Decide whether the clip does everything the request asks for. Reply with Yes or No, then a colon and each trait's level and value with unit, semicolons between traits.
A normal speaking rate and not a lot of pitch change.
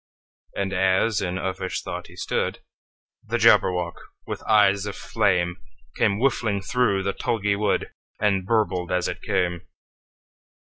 No: slow, 115 wpm; narrow, 2.2 semitones